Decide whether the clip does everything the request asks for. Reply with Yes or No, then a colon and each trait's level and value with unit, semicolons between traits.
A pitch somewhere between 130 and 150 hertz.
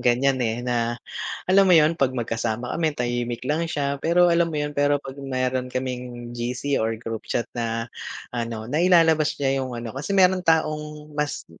Yes: low, 135 Hz